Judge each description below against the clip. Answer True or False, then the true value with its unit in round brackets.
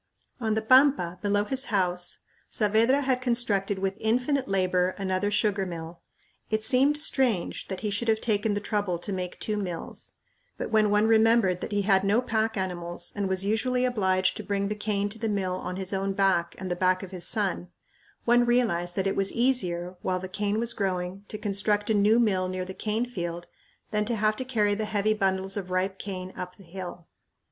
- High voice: True (200 Hz)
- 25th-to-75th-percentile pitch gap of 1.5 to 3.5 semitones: True (2.9 semitones)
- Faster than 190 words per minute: True (205 wpm)